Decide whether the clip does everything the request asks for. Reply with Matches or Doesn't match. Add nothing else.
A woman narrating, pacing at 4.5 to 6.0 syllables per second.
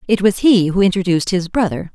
Doesn't match